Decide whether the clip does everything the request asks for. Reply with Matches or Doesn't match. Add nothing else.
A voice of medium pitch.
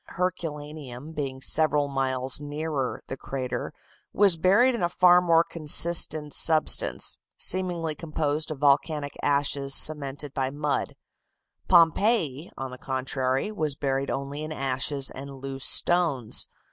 Matches